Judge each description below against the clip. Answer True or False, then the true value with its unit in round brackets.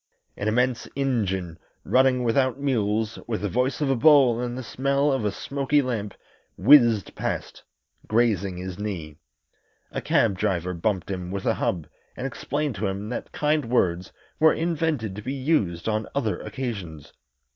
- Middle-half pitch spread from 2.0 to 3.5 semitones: False (5.5 semitones)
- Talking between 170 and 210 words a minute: False (160 wpm)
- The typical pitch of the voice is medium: False (115 Hz)